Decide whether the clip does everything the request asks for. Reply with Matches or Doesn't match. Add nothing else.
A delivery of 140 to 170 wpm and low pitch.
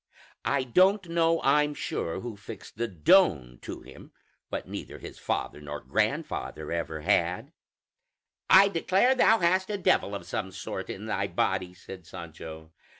Matches